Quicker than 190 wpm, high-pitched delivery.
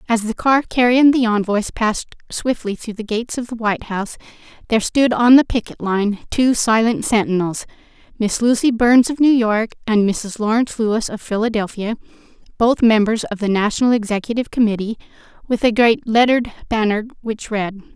No: average, 165 wpm; high, 225 Hz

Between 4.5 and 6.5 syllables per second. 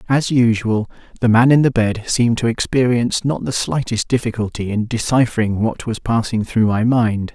Yes: 5.1 syllables/s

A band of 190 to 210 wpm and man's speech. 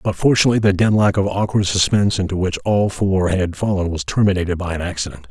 Yes: fast, 205 wpm; male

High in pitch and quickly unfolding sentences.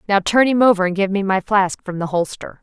Yes: high, 195 Hz; fast, 275 wpm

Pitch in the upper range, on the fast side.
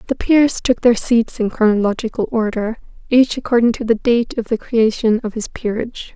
No: high, 230 Hz; average, 185 wpm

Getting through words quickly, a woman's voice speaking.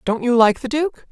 Yes: fast, 270 wpm; female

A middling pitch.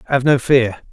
No: low, 130 Hz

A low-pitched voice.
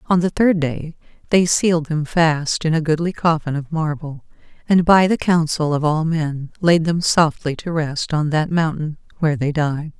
No: medium, 160 Hz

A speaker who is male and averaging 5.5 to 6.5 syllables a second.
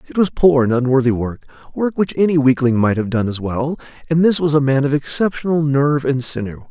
Yes: male; 5.7 syllables/s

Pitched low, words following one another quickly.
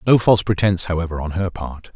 Yes: very low, 90 Hz; fast, 215 wpm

